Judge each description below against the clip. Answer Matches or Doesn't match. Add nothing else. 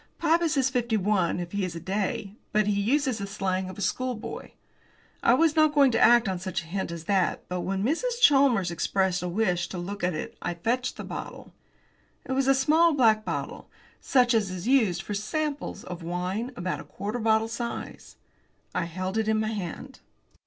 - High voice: Matches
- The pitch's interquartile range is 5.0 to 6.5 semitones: Matches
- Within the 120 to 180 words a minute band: Doesn't match